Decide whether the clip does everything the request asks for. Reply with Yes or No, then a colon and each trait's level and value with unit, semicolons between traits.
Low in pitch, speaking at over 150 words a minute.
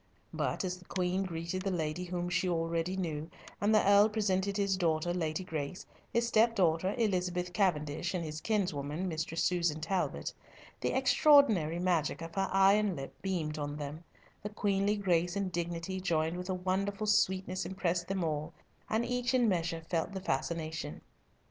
No: medium, 180 Hz; average, 165 wpm